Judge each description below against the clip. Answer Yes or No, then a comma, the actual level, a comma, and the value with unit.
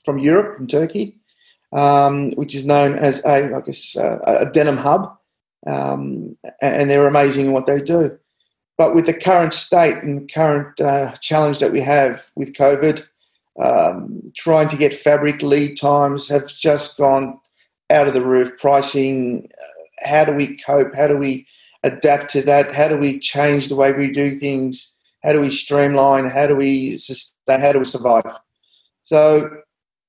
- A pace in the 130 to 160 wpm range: No, average, 170 wpm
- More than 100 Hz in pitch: Yes, medium, 140 Hz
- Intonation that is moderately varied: No, narrow, 1.4 semitones